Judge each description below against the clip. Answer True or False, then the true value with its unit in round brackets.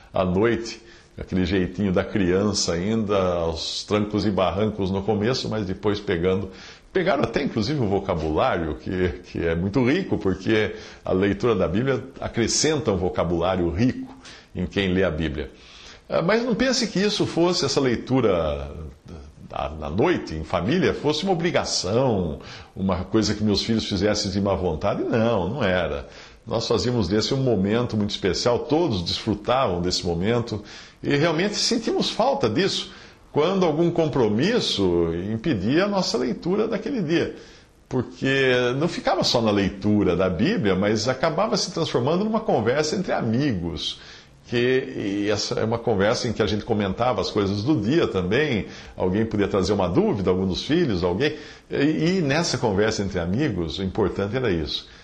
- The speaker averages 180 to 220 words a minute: False (155 wpm)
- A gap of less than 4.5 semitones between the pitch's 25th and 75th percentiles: False (5.1 semitones)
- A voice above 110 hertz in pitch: False (105 Hz)